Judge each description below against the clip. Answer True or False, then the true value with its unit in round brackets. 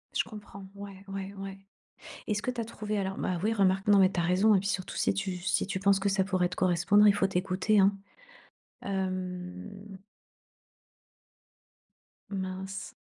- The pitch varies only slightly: True (1.4 semitones)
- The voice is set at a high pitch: True (195 Hz)